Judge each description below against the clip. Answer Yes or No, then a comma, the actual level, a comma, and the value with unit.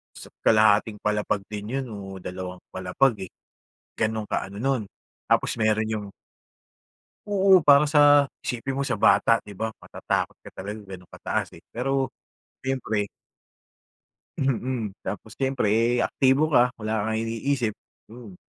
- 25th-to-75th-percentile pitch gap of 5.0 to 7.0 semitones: No, average, 4.2 semitones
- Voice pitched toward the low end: Yes, low, 110 Hz